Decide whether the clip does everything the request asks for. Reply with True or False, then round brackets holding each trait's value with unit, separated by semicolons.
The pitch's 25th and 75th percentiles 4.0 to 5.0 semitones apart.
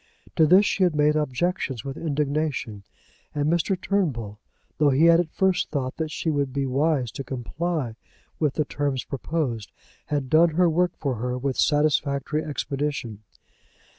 False (3.5 semitones)